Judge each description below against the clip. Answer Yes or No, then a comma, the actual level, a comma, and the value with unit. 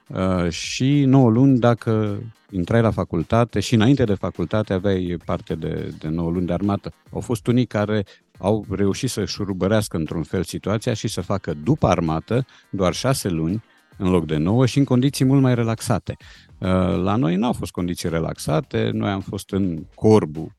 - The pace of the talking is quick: Yes, fast, 180 wpm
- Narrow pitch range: No, average, 4.6 semitones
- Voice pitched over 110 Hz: No, low, 100 Hz